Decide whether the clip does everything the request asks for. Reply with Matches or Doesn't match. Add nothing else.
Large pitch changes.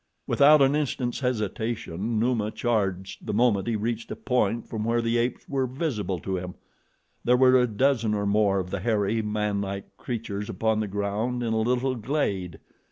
Doesn't match